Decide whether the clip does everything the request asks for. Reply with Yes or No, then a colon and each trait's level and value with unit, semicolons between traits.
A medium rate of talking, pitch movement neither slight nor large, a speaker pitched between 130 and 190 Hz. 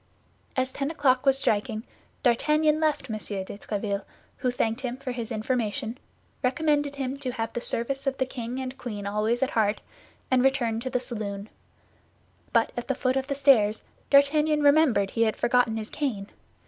No: average, 175 wpm; average, 3.6 semitones; very high, 250 Hz